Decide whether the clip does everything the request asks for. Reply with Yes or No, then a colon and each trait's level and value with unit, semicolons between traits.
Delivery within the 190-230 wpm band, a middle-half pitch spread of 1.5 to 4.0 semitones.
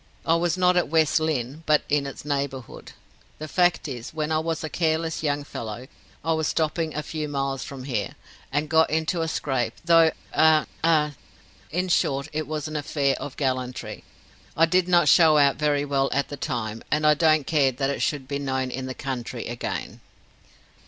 Yes: average, 195 wpm; average, 2.8 semitones